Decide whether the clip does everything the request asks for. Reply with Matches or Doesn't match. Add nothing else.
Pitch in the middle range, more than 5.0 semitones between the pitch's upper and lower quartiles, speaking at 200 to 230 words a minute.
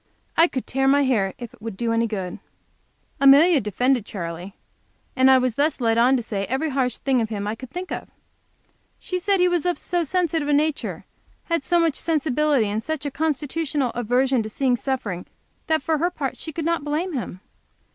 Doesn't match